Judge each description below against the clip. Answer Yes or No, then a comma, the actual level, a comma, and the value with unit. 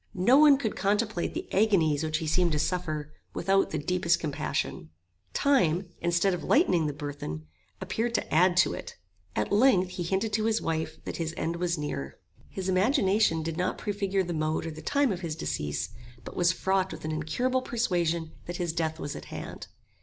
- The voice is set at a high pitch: No, medium, 175 Hz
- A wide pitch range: No, average, 4.0 semitones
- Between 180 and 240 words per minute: Yes, average, 190 wpm